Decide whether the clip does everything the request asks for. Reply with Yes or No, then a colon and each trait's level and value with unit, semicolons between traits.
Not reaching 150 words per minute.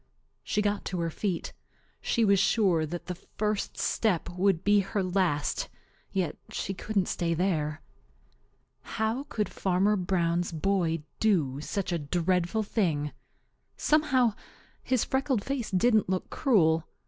Yes: slow, 135 wpm